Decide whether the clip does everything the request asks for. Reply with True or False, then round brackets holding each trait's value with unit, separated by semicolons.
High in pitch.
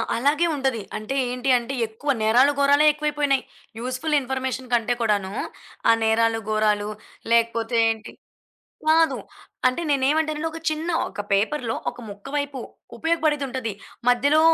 True (260 Hz)